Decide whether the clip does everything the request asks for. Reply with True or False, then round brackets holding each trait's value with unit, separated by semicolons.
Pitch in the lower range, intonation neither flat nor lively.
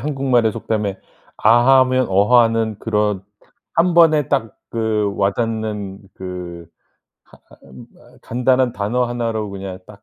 True (110 Hz; 3.7 semitones)